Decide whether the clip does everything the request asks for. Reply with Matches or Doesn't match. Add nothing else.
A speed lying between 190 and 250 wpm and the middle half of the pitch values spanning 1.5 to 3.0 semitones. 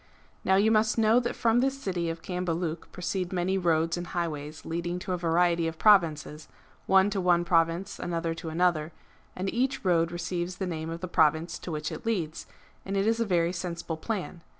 Matches